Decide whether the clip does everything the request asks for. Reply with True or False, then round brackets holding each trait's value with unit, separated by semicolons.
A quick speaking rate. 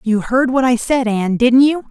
True (250 wpm)